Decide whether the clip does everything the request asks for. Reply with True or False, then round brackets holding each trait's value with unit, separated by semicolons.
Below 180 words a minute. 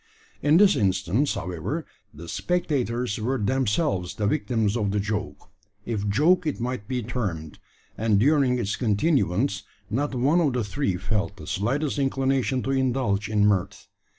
True (150 wpm)